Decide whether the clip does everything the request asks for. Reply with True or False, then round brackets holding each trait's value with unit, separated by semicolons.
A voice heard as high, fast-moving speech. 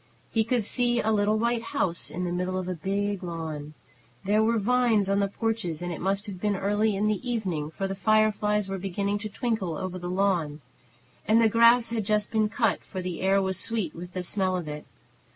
True (200 Hz; 220 wpm)